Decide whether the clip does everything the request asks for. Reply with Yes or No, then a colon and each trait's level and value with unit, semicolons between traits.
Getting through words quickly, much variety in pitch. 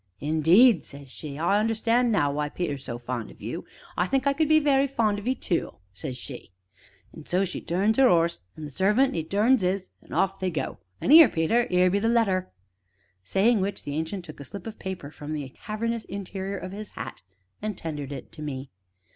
Yes: fast, 215 wpm; wide, 6.5 semitones